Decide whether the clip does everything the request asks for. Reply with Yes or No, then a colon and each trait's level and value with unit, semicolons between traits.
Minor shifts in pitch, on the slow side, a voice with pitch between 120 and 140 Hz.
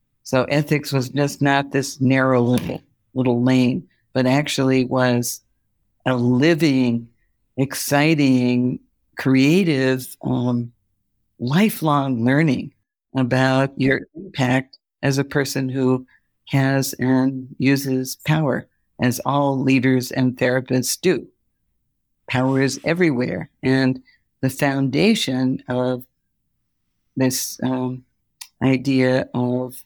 Yes: narrow, 1.4 semitones; slow, 95 wpm; low, 130 Hz